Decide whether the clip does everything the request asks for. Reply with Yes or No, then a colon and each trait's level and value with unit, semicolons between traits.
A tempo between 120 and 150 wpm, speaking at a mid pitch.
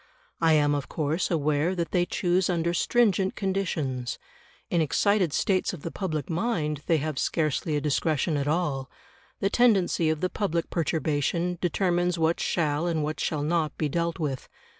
No: average, 165 wpm; medium, 165 Hz